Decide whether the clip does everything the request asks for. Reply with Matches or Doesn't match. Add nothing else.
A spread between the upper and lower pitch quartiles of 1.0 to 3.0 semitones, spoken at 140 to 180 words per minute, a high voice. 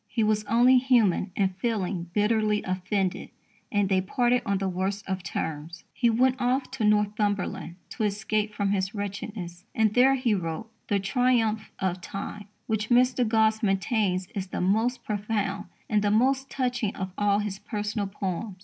Matches